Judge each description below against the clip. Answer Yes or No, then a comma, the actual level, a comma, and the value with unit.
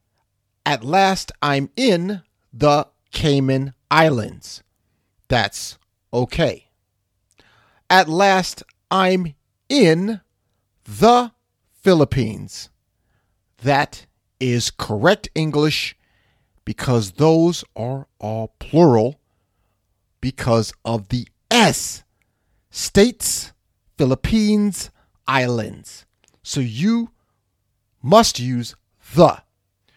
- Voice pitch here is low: Yes, low, 120 Hz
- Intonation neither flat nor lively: No, wide, 7.3 semitones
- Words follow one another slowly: Yes, slow, 70 wpm